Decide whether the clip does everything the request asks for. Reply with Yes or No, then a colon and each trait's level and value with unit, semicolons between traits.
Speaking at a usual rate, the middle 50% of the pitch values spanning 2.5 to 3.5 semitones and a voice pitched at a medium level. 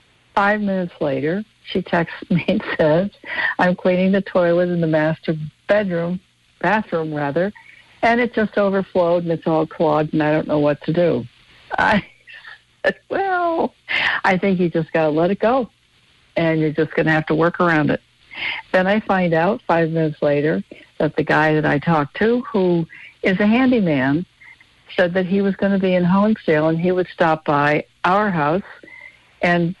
No: average, 180 wpm; average, 4.1 semitones; medium, 180 Hz